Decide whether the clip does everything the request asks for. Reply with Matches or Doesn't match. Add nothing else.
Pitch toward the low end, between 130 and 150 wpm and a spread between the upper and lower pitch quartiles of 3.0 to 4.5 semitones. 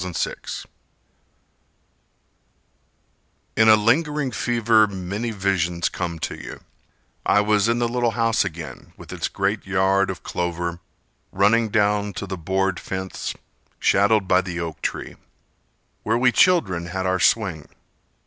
Matches